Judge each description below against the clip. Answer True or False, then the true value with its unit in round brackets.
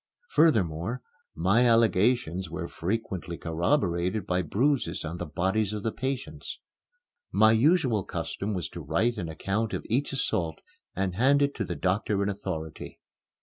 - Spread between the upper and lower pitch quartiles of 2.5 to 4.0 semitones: False (5.1 semitones)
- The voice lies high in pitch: False (100 Hz)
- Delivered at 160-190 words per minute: False (150 wpm)